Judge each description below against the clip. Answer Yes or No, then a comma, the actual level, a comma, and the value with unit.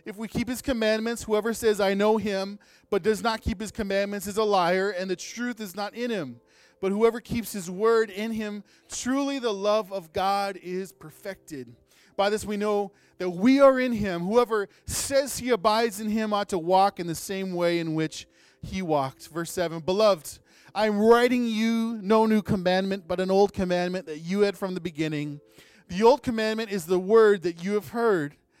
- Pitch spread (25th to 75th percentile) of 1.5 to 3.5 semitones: Yes, average, 3.2 semitones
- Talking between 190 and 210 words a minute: Yes, average, 200 wpm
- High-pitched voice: Yes, high, 205 Hz